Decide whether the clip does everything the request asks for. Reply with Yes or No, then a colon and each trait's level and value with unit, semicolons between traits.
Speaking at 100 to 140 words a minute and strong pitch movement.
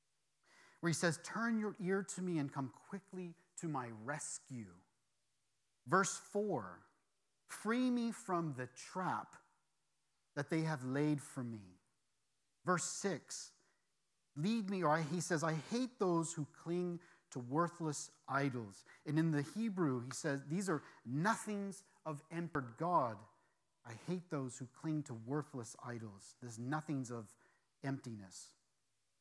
Yes: slow, 135 wpm; wide, 5.8 semitones